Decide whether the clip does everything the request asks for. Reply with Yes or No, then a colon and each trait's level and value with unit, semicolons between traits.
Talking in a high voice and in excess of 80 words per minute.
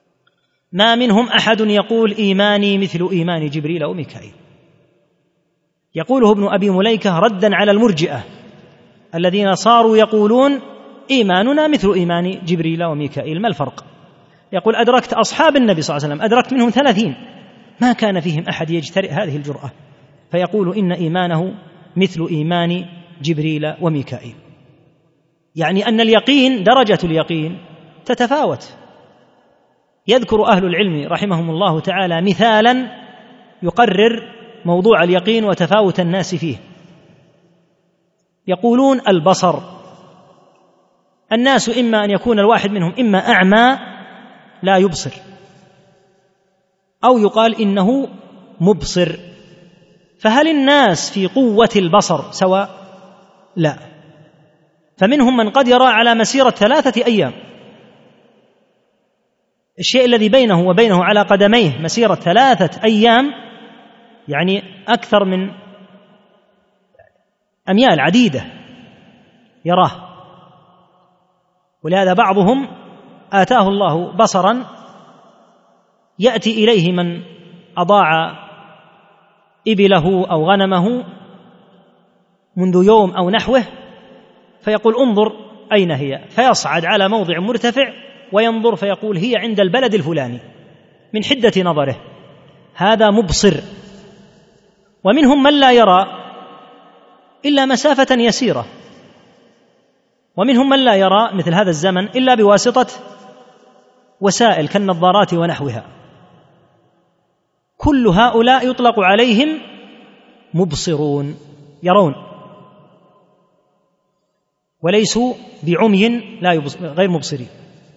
Yes: high, 195 Hz; average, 95 wpm